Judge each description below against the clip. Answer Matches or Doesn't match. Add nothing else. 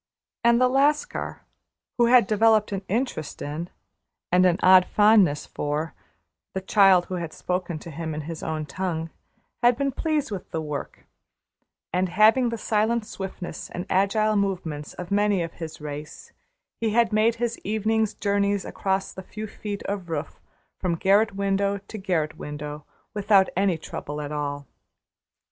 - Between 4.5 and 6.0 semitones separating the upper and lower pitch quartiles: Matches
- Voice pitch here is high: Matches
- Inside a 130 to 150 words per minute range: Doesn't match